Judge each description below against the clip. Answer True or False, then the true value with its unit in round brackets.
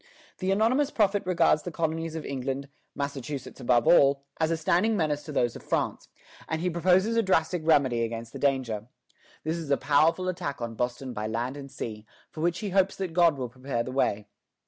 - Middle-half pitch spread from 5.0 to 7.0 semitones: True (5.3 semitones)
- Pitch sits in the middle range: True (150 Hz)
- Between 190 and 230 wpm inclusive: True (200 wpm)